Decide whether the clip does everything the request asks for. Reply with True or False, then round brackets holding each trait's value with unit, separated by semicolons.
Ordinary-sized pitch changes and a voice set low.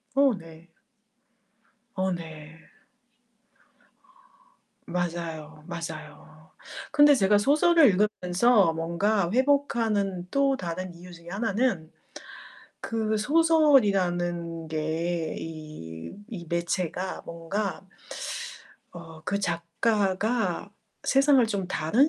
False (4.9 semitones; 185 Hz)